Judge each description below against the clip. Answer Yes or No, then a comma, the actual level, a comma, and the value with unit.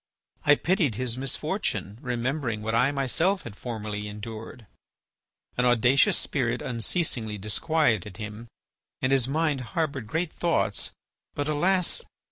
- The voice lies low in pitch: Yes, low, 125 Hz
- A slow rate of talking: Yes, slow, 120 wpm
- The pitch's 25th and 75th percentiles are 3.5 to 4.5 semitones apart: No, average, 5.3 semitones